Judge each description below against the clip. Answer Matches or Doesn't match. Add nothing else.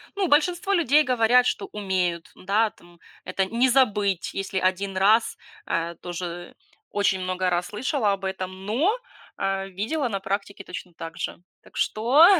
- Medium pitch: Doesn't match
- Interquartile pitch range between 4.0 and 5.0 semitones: Matches